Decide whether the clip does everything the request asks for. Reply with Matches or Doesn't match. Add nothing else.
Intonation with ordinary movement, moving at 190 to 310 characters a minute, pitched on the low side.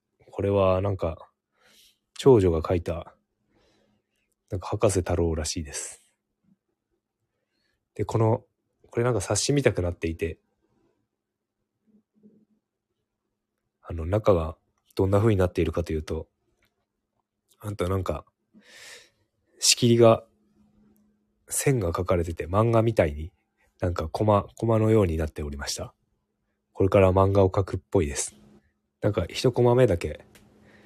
Matches